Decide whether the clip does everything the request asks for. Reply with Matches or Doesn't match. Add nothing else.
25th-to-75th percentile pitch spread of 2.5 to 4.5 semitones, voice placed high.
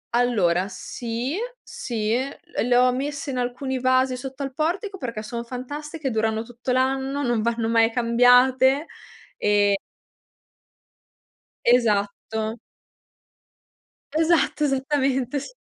Matches